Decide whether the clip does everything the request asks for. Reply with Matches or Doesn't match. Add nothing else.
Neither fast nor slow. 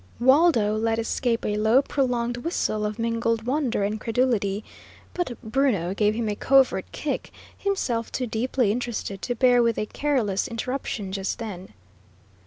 Matches